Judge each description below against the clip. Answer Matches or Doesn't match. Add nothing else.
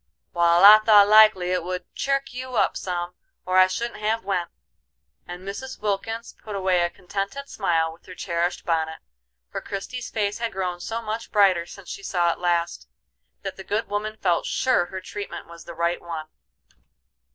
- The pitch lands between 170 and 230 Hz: Matches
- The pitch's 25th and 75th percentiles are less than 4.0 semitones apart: Matches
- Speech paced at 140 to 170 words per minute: Doesn't match